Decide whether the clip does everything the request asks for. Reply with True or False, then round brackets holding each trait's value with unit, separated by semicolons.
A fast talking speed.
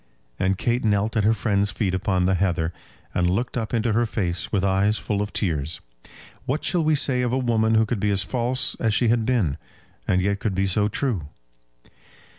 True (210 wpm)